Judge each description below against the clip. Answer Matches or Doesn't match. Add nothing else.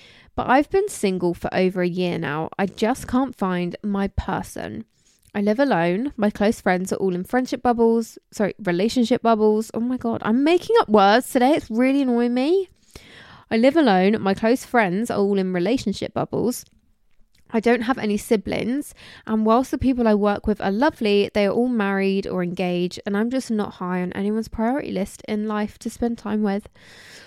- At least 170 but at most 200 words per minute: Matches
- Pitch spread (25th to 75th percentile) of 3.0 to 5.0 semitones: Matches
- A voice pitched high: Matches